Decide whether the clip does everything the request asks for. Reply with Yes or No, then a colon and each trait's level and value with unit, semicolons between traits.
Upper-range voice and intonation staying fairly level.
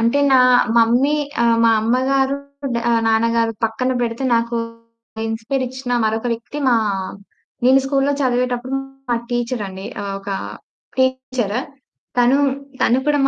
Yes: high, 245 Hz; narrow, 2.3 semitones